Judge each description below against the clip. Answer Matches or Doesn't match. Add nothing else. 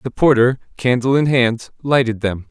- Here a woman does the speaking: Doesn't match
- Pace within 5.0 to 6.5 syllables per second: Doesn't match